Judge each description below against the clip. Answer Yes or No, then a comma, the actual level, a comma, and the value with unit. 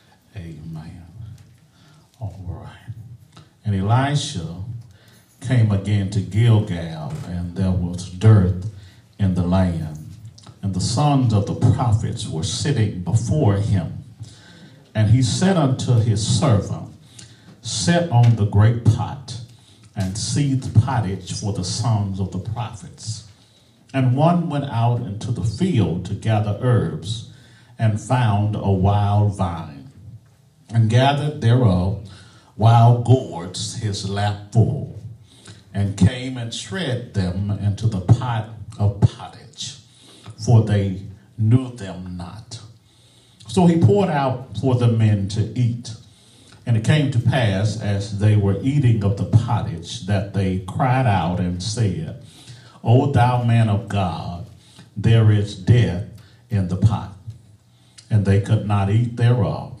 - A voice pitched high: No, low, 110 Hz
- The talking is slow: Yes, slow, 130 wpm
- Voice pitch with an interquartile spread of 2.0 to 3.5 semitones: Yes, average, 3.2 semitones